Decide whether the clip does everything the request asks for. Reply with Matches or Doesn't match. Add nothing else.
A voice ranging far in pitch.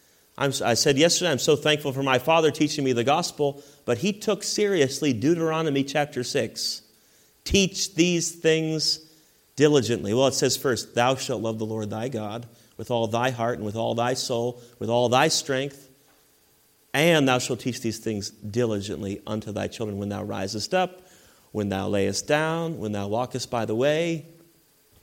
Matches